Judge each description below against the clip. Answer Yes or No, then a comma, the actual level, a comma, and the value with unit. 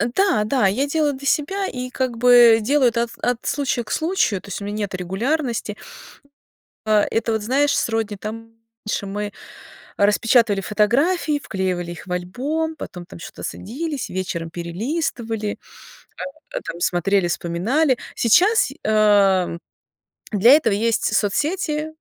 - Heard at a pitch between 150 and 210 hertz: No, high, 225 Hz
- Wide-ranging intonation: Yes, wide, 6.0 semitones